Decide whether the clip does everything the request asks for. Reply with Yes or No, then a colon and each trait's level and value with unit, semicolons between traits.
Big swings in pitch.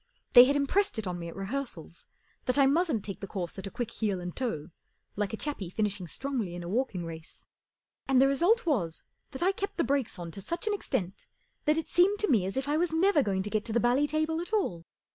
Yes: wide, 8.0 semitones